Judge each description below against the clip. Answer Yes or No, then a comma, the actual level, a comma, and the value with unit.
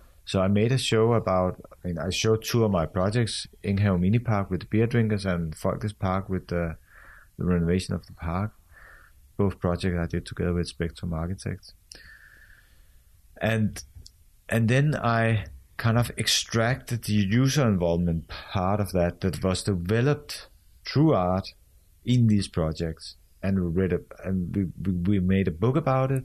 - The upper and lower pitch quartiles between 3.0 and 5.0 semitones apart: Yes, average, 4.2 semitones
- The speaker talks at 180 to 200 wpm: No, average, 160 wpm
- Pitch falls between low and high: No, very low, 95 Hz